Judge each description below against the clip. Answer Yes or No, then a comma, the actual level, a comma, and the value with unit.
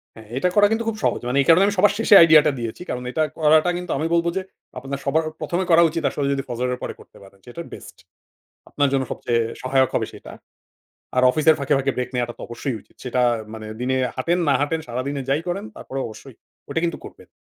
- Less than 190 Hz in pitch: Yes, medium, 140 Hz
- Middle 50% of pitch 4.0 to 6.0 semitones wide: Yes, average, 4.6 semitones